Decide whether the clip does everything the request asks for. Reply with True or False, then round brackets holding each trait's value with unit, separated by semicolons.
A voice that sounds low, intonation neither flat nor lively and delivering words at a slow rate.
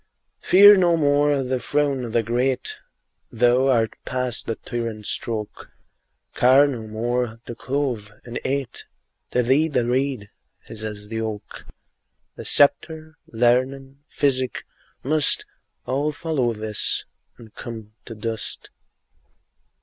True (125 Hz; 3.7 semitones; 125 wpm)